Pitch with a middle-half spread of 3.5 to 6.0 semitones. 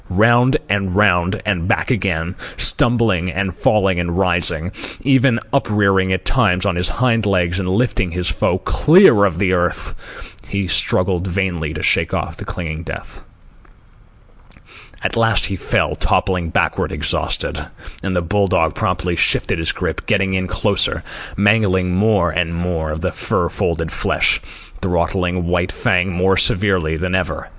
No: narrow, 2.6 semitones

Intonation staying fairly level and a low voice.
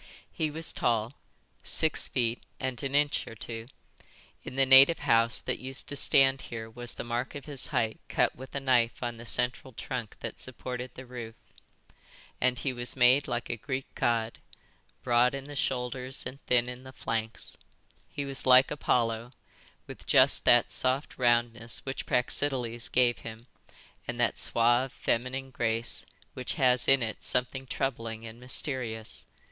Yes: narrow, 2.2 semitones; low, 125 Hz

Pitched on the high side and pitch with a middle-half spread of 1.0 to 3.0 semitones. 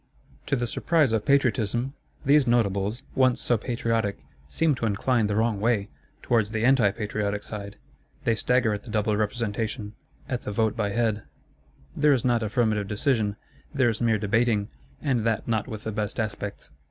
No: low, 110 Hz; narrow, 2.6 semitones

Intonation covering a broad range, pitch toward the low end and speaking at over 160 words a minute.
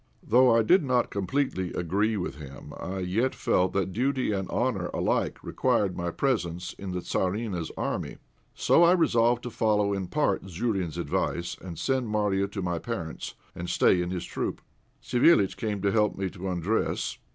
No: average, 4.7 semitones; low, 100 Hz; average, 175 wpm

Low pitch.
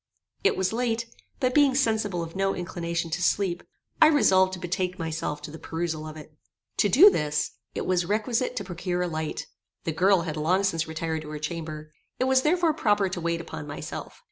No: medium, 180 Hz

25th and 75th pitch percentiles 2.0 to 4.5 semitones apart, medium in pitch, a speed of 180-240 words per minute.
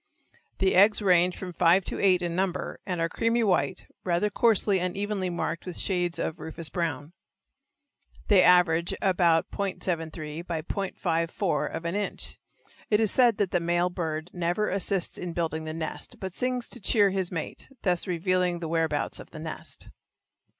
No: narrow, 2.6 semitones; medium, 180 Hz; average, 170 wpm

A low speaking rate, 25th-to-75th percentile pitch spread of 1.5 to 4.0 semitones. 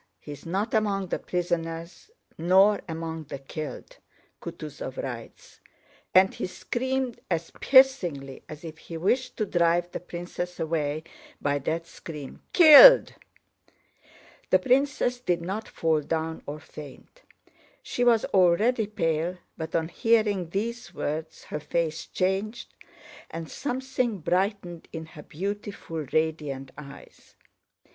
No: slow, 120 wpm; average, 5.2 semitones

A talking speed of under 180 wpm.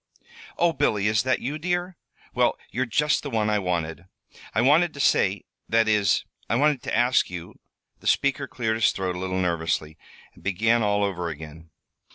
No: average, 190 wpm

